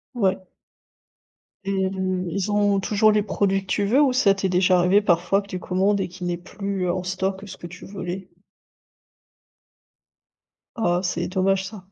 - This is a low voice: No, high, 190 Hz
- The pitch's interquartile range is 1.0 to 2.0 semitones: Yes, narrow, 1.6 semitones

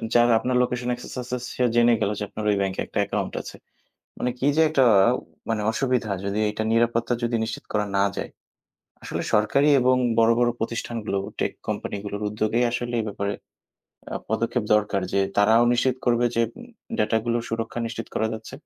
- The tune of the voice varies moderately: No, narrow, 2.2 semitones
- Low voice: Yes, low, 115 Hz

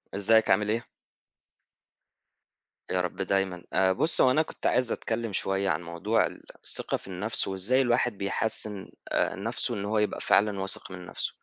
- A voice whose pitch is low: Yes, low, 100 Hz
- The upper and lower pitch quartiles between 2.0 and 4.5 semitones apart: Yes, average, 3.0 semitones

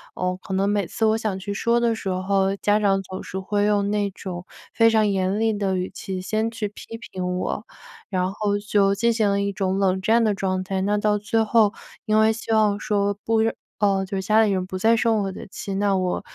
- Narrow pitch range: Yes, narrow, 2.2 semitones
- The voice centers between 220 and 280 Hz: No, high, 200 Hz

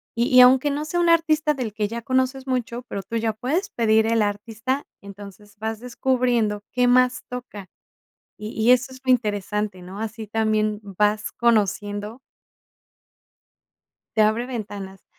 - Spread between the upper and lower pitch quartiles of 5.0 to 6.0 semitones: No, average, 3.3 semitones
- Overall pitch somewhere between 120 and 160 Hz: No, high, 225 Hz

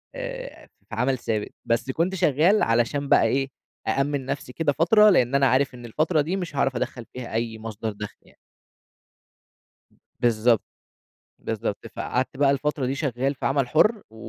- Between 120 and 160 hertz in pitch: Yes, low, 135 Hz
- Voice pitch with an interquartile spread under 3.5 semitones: No, average, 4.3 semitones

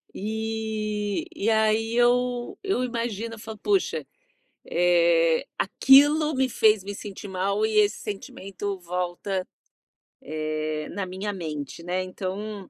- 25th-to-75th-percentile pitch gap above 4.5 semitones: No, average, 3.5 semitones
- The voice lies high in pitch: Yes, high, 205 Hz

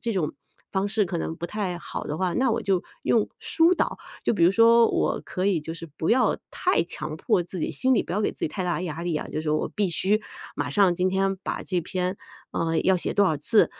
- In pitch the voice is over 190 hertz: No, medium, 185 Hz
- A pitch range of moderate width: Yes, average, 3.7 semitones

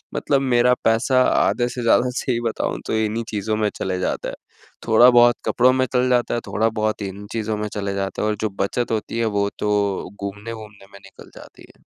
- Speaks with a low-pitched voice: Yes, low, 110 Hz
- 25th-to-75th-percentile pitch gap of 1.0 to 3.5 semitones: Yes, average, 2.8 semitones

